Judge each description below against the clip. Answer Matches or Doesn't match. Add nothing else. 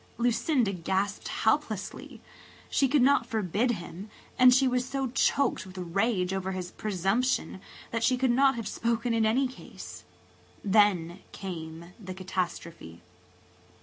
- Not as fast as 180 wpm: Matches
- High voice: Matches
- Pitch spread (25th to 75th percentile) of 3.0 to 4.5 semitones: Doesn't match